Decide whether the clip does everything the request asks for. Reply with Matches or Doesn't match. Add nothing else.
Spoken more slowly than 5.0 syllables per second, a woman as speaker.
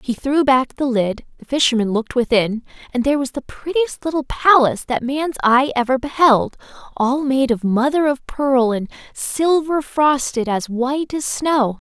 Matches